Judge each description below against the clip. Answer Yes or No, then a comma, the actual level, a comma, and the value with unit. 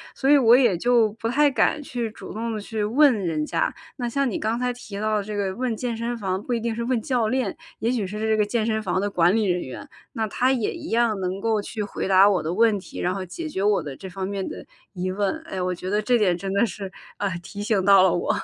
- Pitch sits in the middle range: No, high, 215 Hz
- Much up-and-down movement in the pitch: No, average, 3.5 semitones